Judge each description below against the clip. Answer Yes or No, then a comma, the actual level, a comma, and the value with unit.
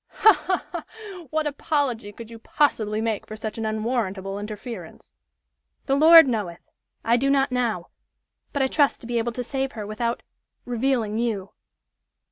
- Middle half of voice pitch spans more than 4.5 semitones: No, average, 4.2 semitones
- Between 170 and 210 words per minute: No, average, 160 wpm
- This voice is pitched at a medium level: No, high, 235 Hz